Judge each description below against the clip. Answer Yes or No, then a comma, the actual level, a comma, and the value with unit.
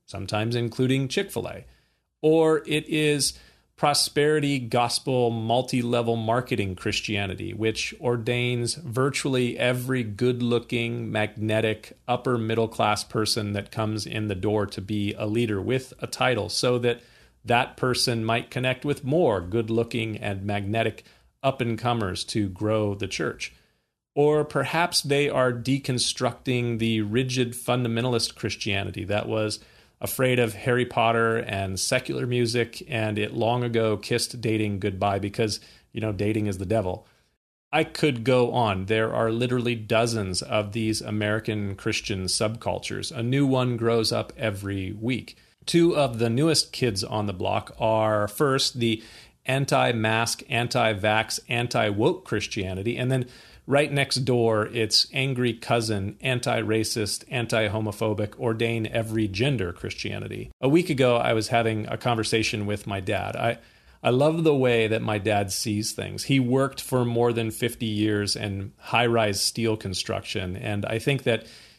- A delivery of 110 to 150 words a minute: Yes, average, 145 wpm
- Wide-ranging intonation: No, narrow, 2.6 semitones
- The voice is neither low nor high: No, low, 115 Hz